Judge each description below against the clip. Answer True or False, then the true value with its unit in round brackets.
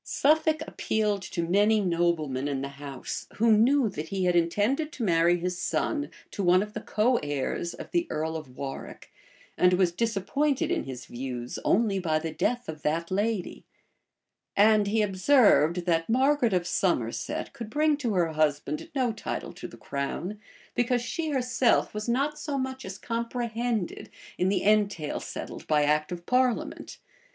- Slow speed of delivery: False (165 wpm)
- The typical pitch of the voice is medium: False (200 Hz)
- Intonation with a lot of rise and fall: True (6.5 semitones)